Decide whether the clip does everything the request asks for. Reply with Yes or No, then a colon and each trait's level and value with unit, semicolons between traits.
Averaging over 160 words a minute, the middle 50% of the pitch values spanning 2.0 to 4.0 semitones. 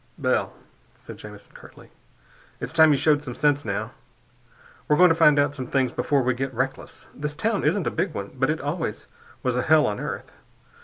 Yes: average, 200 wpm; average, 3.3 semitones